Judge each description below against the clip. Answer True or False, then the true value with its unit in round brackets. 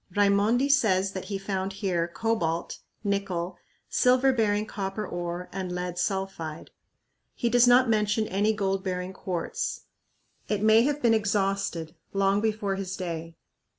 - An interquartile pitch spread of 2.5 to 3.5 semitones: True (2.9 semitones)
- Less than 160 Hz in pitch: False (195 Hz)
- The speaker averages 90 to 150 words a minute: True (140 wpm)